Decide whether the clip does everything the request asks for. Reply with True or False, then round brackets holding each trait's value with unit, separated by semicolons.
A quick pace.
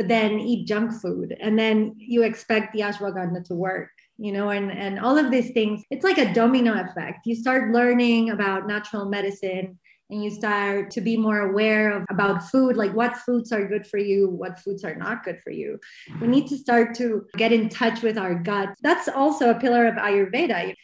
True (215 wpm)